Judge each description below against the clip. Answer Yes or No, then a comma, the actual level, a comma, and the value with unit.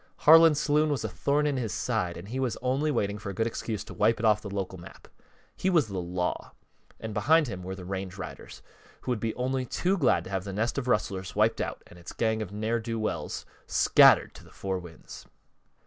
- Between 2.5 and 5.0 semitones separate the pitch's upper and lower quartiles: No, wide, 5.5 semitones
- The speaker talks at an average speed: No, fast, 230 wpm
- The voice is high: No, low, 110 Hz